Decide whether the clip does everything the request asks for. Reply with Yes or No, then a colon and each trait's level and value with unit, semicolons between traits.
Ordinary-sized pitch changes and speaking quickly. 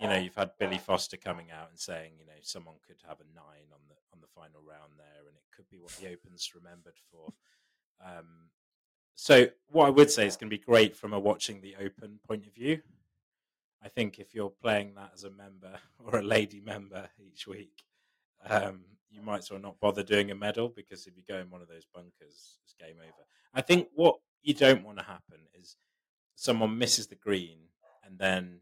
Yes: average, 3.4 semitones; fast, 220 wpm